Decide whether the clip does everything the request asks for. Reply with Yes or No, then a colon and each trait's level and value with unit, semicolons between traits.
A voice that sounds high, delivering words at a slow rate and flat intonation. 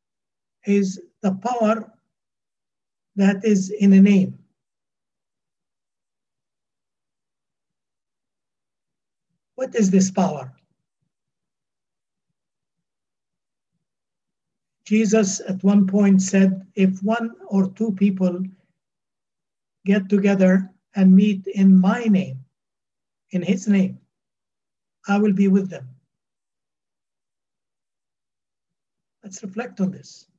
Yes: high, 195 Hz; slow, 80 wpm; narrow, 1.6 semitones